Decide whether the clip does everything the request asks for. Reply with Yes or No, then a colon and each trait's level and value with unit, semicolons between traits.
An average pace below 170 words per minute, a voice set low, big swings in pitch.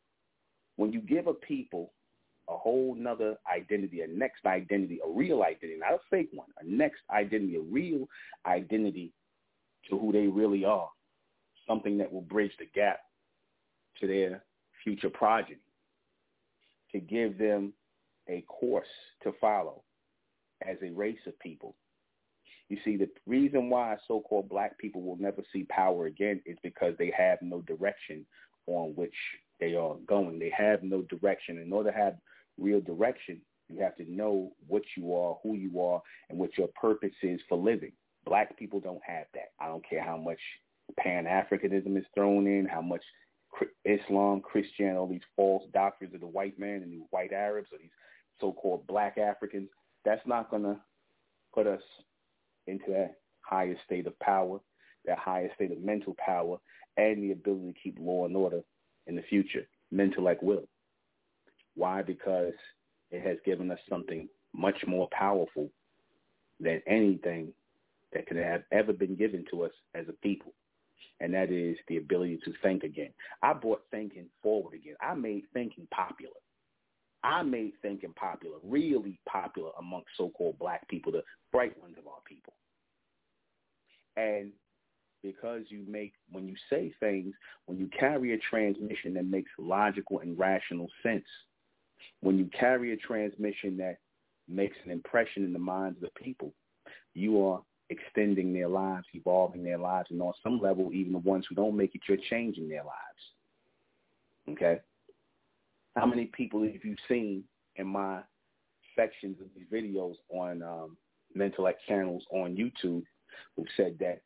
No: average, 160 wpm; low, 100 Hz; narrow, 2.4 semitones